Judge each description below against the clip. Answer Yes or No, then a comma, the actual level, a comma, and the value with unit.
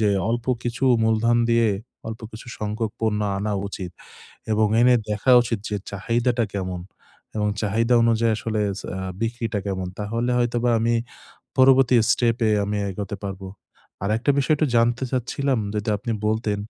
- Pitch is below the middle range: Yes, low, 115 Hz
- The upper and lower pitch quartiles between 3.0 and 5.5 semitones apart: No, narrow, 2.4 semitones